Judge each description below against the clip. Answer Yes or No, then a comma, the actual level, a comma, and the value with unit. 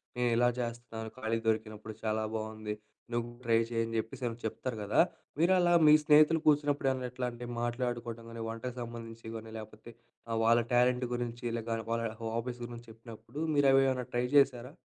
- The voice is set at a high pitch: No, low, 120 Hz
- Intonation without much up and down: Yes, narrow, 1.9 semitones